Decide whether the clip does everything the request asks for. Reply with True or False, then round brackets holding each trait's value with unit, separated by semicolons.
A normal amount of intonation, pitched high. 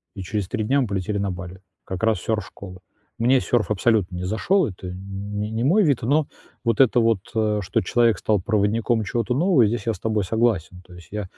False (3.5 semitones; 105 Hz)